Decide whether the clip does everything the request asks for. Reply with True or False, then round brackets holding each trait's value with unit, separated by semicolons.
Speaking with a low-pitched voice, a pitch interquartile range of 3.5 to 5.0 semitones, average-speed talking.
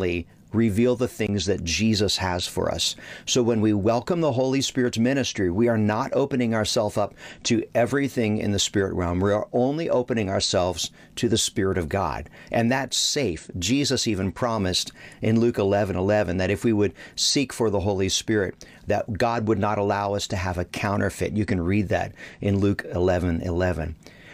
True (105 Hz; 4.0 semitones; 185 wpm)